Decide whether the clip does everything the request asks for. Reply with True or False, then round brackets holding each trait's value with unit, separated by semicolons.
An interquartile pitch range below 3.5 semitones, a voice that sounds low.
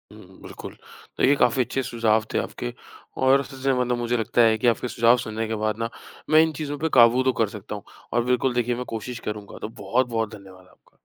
True (2.4 semitones; 120 Hz)